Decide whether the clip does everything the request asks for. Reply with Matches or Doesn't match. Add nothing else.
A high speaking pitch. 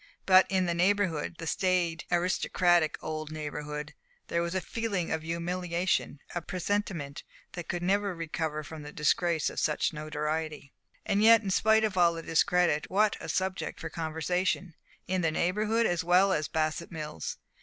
Doesn't match